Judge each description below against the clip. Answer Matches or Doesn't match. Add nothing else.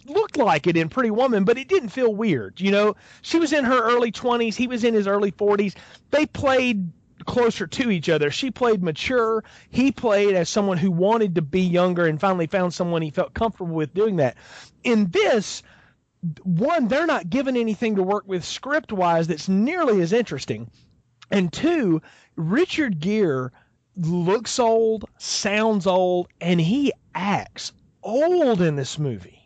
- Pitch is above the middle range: Matches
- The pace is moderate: Matches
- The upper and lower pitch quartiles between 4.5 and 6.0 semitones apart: Matches